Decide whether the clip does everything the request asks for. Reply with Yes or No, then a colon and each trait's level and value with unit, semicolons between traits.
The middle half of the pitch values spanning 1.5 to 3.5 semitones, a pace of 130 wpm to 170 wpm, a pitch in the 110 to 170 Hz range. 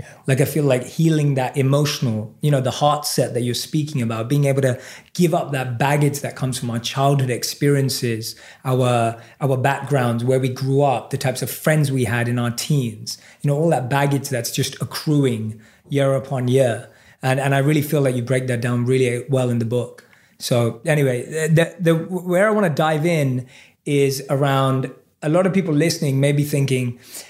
No: average, 2.9 semitones; average, 200 wpm; low, 135 Hz